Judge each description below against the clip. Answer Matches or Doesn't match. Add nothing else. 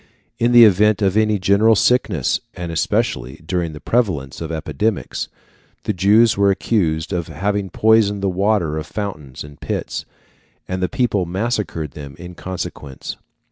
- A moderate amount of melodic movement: Matches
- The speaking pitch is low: Matches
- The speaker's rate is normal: Matches